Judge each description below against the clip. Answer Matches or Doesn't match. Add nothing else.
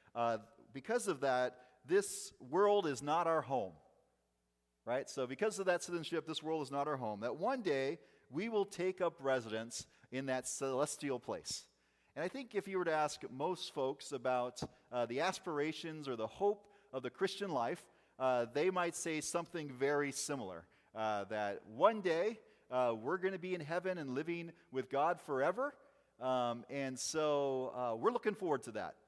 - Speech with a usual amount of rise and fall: Doesn't match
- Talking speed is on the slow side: Doesn't match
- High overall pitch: Doesn't match